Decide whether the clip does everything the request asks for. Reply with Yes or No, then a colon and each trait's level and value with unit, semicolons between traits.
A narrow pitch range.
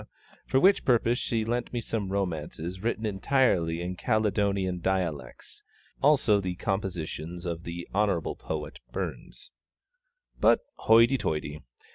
No: average, 4.6 semitones